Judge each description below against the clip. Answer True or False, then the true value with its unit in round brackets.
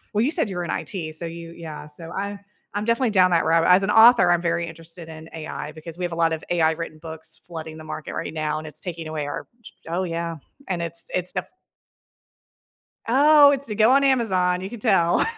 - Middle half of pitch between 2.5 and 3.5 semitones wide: False (4.0 semitones)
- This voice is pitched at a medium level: True (170 Hz)